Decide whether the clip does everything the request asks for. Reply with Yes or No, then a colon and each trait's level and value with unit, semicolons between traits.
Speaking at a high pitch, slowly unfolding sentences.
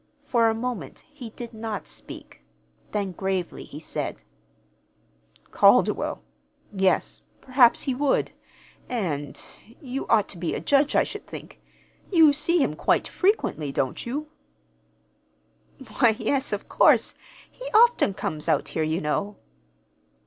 Yes: high, 230 Hz; slow, 130 wpm